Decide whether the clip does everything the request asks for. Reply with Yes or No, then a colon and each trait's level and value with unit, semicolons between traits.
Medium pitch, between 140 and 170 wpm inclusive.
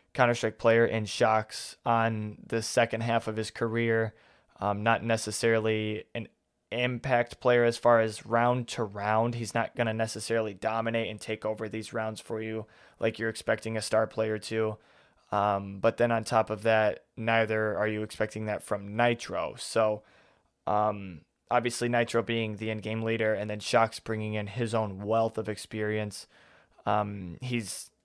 No: low, 110 Hz; average, 165 wpm